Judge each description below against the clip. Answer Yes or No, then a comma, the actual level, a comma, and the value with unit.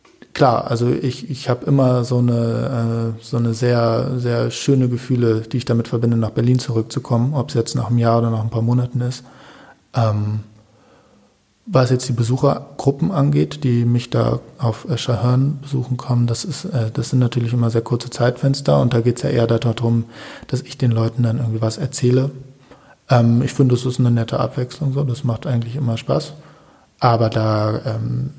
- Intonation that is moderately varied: No, narrow, 2.0 semitones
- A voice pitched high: No, low, 120 Hz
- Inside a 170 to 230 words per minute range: Yes, average, 175 wpm